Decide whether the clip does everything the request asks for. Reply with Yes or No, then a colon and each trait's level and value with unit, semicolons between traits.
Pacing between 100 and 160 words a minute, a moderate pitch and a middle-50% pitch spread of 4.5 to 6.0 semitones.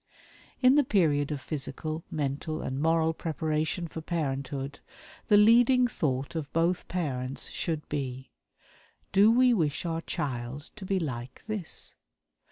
Yes: slow, 135 wpm; medium, 155 Hz; average, 4.8 semitones